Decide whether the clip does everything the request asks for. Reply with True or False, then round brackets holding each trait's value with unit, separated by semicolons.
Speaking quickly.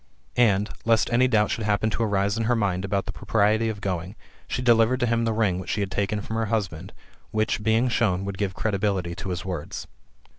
True (220 wpm)